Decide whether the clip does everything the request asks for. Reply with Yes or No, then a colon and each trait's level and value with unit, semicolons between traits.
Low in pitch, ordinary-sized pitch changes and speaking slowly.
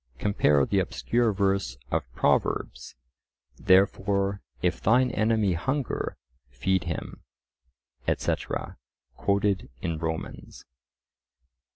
Yes: low, 100 Hz; average, 3.6 semitones; slow, 85 wpm